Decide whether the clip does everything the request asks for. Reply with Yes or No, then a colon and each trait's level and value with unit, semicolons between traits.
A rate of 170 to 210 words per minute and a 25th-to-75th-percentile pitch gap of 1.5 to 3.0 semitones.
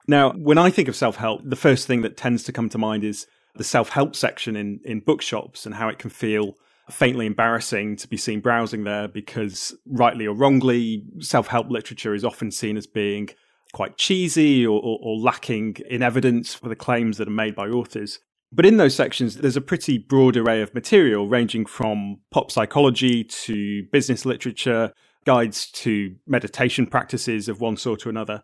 Yes: average, 190 wpm; narrow, 2.6 semitones